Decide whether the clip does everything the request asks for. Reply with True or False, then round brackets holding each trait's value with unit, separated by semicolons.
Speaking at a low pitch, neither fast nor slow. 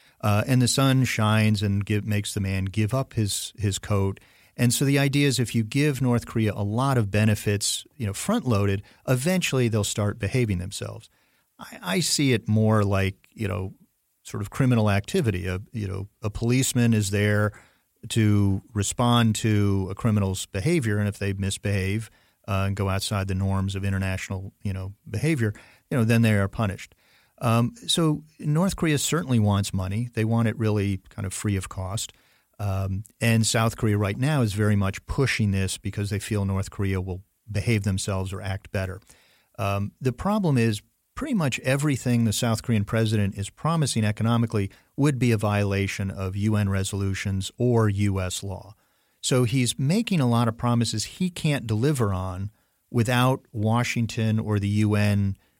True (105 Hz; 175 wpm)